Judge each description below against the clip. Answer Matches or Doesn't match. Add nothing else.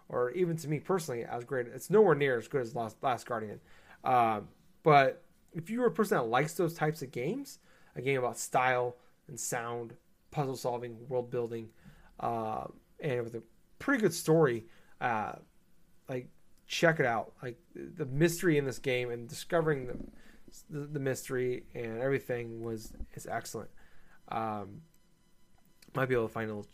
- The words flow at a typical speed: Matches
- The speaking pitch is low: Matches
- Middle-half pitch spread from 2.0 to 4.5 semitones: Doesn't match